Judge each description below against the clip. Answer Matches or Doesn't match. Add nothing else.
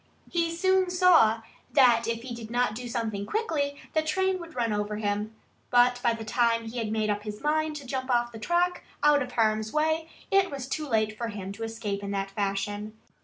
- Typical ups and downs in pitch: Doesn't match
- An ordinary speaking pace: Doesn't match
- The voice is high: Matches